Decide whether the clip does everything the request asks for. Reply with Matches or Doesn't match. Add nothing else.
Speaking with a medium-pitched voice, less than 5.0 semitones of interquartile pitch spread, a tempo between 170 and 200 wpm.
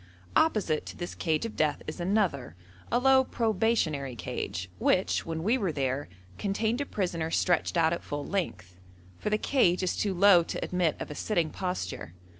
Doesn't match